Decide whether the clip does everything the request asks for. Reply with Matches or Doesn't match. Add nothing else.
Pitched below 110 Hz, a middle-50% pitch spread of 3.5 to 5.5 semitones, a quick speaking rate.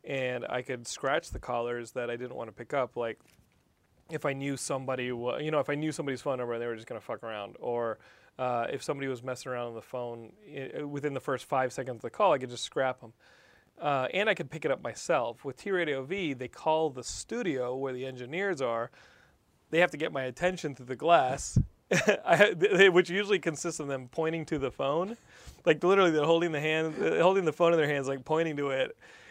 Doesn't match